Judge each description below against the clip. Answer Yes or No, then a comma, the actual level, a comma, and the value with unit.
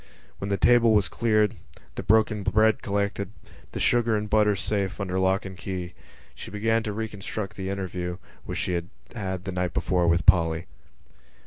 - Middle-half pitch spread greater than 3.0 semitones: No, narrow, 2.6 semitones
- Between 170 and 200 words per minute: Yes, average, 175 wpm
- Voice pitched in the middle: No, low, 100 Hz